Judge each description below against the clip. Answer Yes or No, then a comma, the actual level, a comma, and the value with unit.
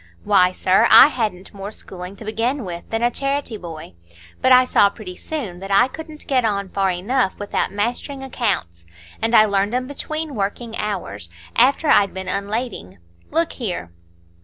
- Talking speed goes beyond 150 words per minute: Yes, average, 170 wpm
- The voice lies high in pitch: Yes, high, 210 Hz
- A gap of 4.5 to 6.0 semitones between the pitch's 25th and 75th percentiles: Yes, average, 5.0 semitones